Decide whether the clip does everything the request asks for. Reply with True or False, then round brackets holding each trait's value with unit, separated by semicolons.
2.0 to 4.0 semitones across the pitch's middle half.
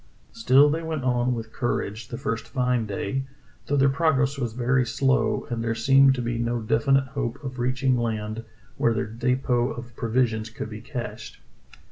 True (2.7 semitones)